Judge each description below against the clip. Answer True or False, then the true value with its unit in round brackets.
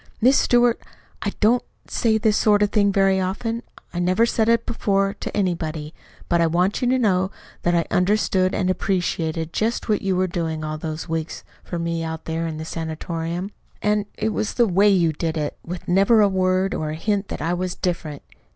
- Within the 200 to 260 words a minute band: True (205 wpm)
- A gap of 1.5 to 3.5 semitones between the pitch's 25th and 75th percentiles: False (4.1 semitones)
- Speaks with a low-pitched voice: False (185 Hz)